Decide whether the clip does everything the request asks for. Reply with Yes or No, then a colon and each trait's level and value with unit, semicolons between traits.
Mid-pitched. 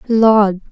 No: high, 210 Hz